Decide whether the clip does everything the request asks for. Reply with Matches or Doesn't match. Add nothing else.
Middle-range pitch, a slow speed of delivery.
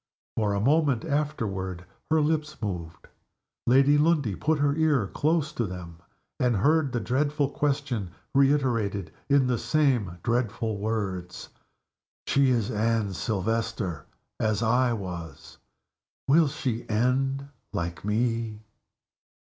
Doesn't match